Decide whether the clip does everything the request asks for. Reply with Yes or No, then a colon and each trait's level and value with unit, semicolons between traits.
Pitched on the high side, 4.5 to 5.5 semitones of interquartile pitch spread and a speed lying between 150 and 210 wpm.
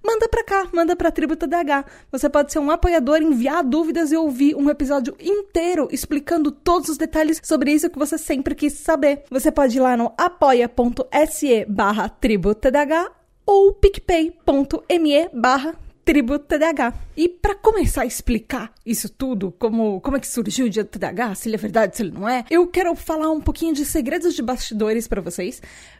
Yes: very high, 295 Hz; average, 5.1 semitones; average, 175 wpm